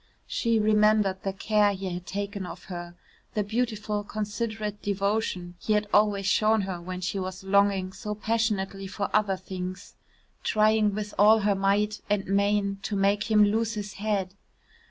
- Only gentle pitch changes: Yes, narrow, 1.7 semitones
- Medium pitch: No, high, 205 Hz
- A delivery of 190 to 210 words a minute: No, average, 160 wpm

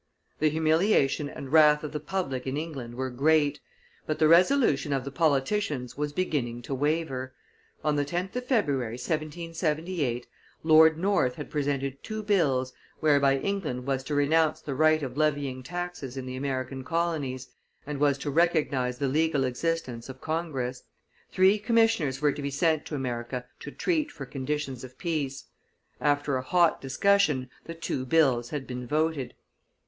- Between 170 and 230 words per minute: No, average, 160 wpm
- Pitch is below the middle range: No, medium, 145 Hz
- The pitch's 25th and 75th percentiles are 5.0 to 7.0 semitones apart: No, average, 3.7 semitones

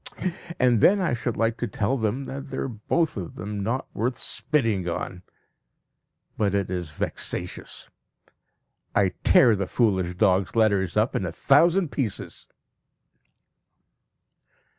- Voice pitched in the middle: No, low, 110 Hz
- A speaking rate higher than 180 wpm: No, slow, 135 wpm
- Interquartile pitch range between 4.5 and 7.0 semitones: Yes, average, 5.1 semitones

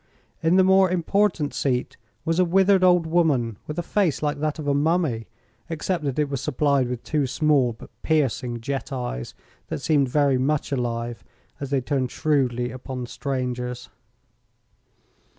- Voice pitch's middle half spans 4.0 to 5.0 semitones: Yes, average, 4.5 semitones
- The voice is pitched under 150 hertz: Yes, medium, 140 Hz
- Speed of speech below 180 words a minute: Yes, average, 165 wpm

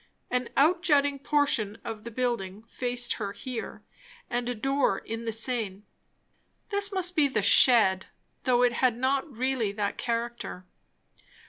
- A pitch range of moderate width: Yes, average, 3.4 semitones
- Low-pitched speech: No, high, 245 Hz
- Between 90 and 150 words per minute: Yes, average, 145 wpm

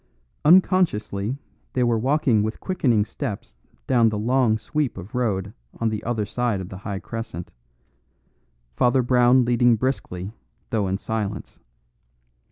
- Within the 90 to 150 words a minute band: Yes, slow, 135 wpm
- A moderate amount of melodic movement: Yes, average, 3.4 semitones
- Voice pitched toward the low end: Yes, low, 115 Hz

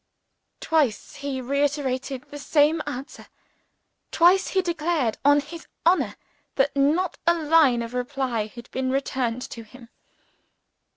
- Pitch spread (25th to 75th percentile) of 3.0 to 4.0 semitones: Yes, average, 3.7 semitones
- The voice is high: Yes, very high, 280 Hz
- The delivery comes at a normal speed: No, slow, 125 wpm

